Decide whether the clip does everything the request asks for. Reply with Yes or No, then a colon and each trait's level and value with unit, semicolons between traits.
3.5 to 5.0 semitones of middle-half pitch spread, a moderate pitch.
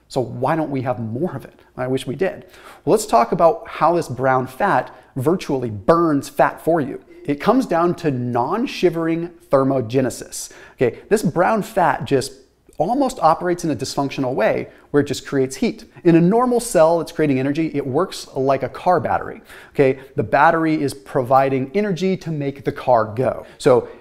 Yes: average, 4.2 semitones; medium, 145 Hz